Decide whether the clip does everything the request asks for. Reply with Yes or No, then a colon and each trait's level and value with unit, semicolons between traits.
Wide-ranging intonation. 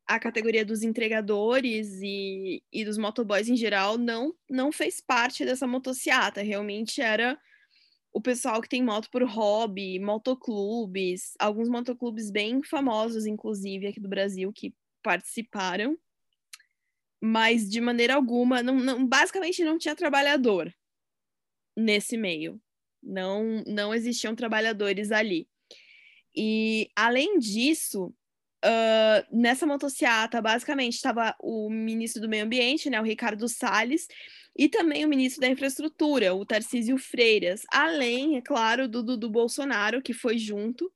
No: average, 4.0 semitones